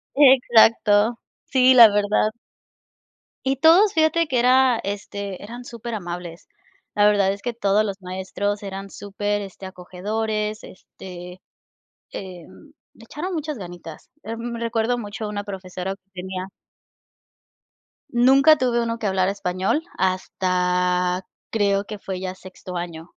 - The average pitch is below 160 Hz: No, high, 205 Hz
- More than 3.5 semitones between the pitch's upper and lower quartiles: Yes, average, 4.1 semitones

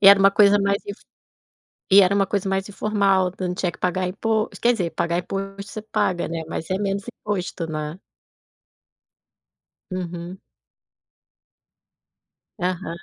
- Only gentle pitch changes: Yes, narrow, 1.9 semitones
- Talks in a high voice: Yes, high, 195 Hz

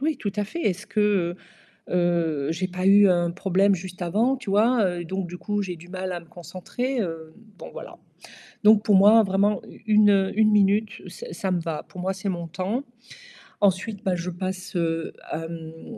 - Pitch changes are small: No, average, 3.0 semitones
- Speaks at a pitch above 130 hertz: Yes, high, 190 Hz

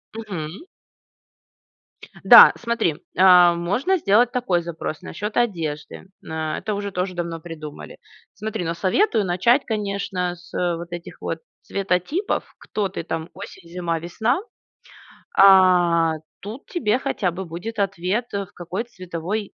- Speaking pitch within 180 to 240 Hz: Yes, medium, 185 Hz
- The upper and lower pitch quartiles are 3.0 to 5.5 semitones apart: Yes, average, 3.7 semitones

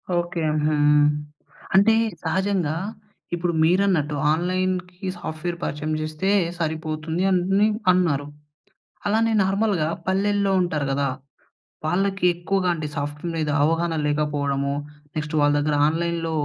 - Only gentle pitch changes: No, average, 3.4 semitones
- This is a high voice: No, medium, 170 Hz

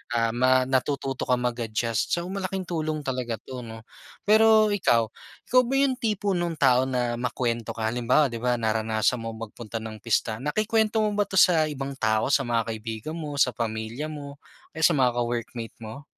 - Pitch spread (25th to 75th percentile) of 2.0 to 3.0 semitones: No, average, 5.3 semitones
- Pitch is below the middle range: Yes, low, 125 Hz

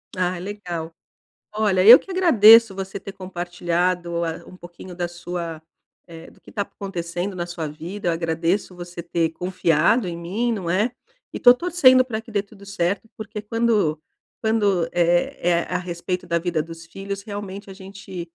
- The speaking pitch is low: No, medium, 185 Hz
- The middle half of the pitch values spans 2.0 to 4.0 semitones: Yes, average, 3.1 semitones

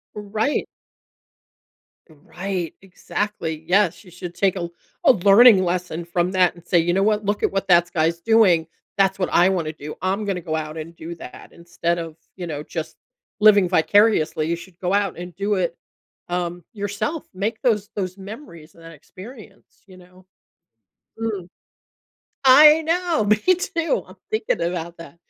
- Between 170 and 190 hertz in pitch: Yes, medium, 185 Hz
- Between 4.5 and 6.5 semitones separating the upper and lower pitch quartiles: No, average, 3.4 semitones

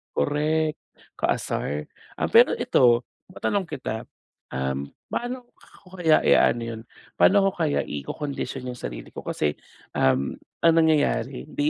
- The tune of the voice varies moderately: No, wide, 5.7 semitones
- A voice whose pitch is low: No, medium, 145 Hz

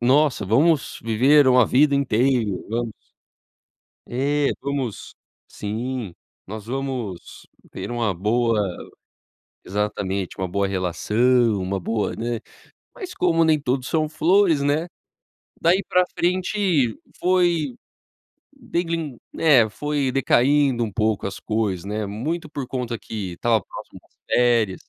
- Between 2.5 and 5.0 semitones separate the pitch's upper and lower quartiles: No, wide, 5.5 semitones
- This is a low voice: Yes, low, 125 Hz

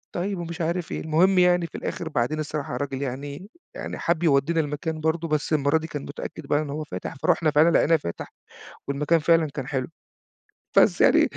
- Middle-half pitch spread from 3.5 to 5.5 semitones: No, average, 2.7 semitones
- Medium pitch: Yes, medium, 155 Hz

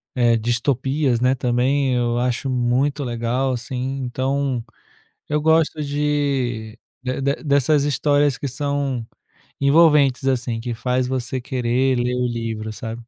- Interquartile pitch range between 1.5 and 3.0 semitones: Yes, average, 2.7 semitones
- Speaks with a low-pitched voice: Yes, low, 130 Hz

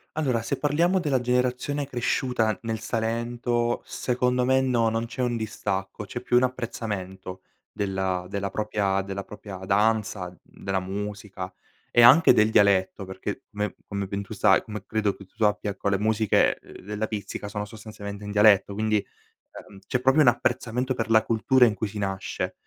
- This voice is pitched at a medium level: No, low, 110 Hz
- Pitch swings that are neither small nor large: Yes, average, 3.4 semitones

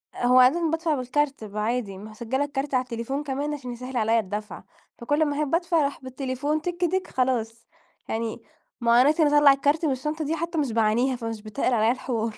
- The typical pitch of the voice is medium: No, very high, 260 Hz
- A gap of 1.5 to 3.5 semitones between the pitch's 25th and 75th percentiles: No, average, 4.2 semitones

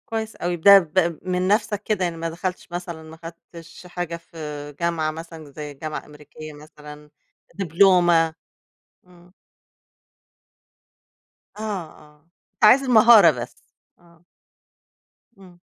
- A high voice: No, medium, 170 Hz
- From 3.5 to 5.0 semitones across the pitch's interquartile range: No, average, 2.8 semitones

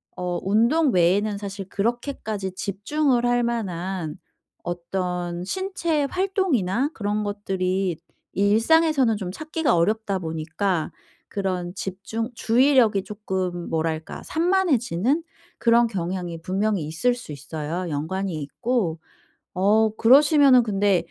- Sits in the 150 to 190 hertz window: No, high, 200 Hz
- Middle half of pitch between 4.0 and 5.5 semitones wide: Yes, average, 5.2 semitones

